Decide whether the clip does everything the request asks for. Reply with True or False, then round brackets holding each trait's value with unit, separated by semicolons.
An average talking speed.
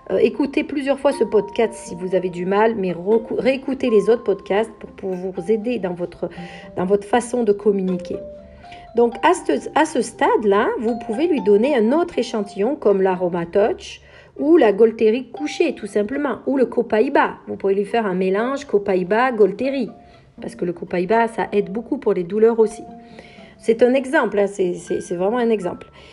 True (185 wpm)